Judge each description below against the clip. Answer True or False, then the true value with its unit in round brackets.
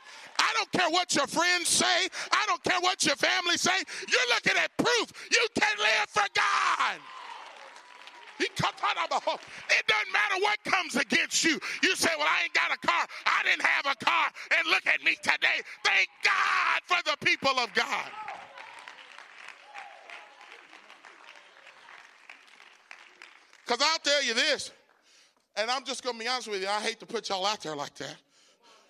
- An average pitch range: False (6.7 semitones)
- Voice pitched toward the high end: True (330 Hz)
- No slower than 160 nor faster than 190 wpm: True (170 wpm)